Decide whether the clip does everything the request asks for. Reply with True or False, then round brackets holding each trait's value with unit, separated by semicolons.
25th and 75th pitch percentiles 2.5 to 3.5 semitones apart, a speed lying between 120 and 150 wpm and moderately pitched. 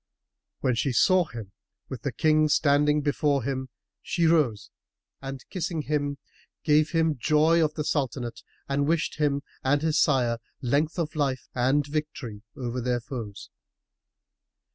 True (3.1 semitones; 140 wpm; 145 Hz)